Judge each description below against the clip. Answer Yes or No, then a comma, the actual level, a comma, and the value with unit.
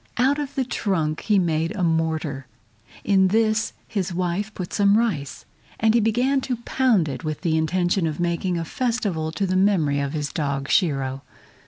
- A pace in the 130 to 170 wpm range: No, average, 180 wpm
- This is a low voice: No, medium, 180 Hz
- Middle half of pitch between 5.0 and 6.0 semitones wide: Yes, wide, 5.4 semitones